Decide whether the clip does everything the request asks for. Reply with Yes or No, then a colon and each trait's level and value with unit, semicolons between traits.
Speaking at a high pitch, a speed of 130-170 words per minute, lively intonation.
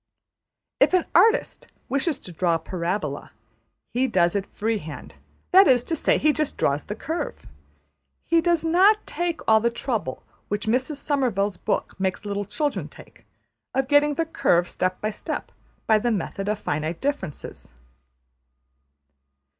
Yes: high, 225 Hz; average, 150 wpm; wide, 8.0 semitones